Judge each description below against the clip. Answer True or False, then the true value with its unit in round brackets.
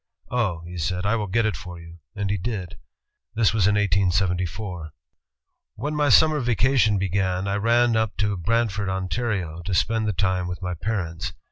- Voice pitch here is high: False (100 Hz)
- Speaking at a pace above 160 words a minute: True (180 wpm)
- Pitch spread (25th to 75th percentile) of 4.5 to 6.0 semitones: False (3.8 semitones)